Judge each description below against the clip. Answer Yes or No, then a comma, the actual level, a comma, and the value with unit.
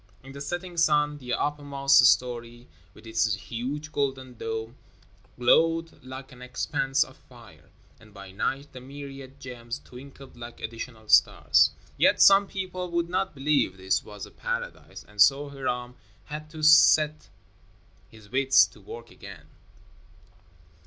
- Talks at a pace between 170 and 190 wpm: No, average, 140 wpm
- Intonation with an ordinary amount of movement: Yes, average, 4.2 semitones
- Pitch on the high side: No, low, 135 Hz